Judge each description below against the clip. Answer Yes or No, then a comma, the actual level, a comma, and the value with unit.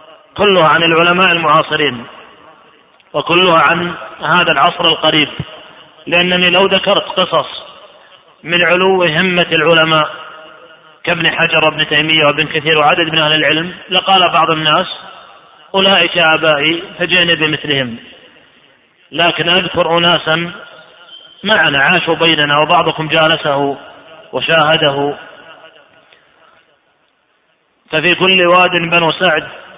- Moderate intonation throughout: No, narrow, 2.0 semitones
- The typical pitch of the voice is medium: Yes, medium, 160 Hz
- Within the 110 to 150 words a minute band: No, average, 95 wpm